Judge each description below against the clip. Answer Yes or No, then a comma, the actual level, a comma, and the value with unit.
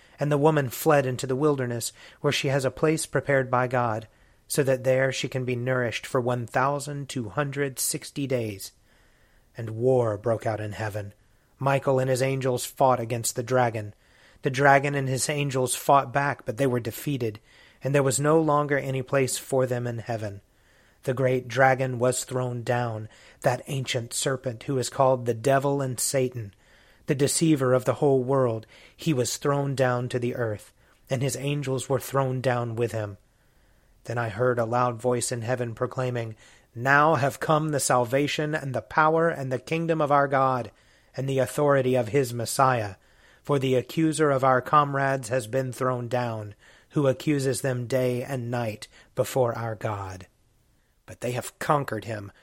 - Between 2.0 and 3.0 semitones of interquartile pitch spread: Yes, narrow, 2.6 semitones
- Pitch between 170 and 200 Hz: No, low, 130 Hz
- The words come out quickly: No, average, 175 wpm